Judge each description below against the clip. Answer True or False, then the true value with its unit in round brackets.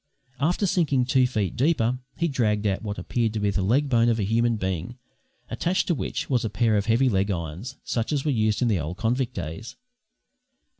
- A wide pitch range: False (4.1 semitones)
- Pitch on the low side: True (115 Hz)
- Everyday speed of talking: False (210 wpm)